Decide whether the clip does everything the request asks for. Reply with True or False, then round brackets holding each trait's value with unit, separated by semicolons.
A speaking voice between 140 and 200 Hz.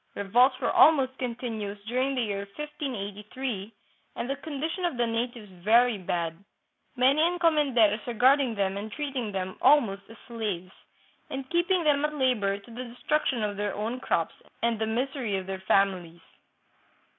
False (235 Hz)